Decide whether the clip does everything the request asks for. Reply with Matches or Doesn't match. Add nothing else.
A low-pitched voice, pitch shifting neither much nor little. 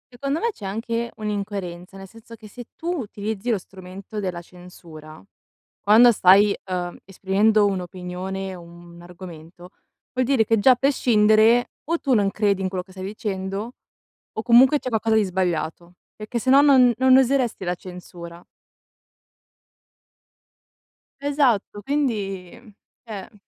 Doesn't match